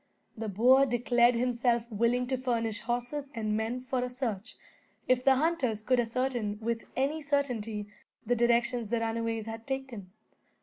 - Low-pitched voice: No, high, 240 Hz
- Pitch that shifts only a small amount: Yes, narrow, 2.2 semitones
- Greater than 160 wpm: No, average, 150 wpm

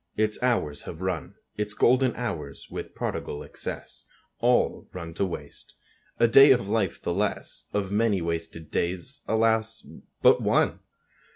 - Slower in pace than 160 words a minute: Yes, average, 145 wpm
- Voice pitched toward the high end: No, low, 105 Hz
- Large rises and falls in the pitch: No, average, 5.0 semitones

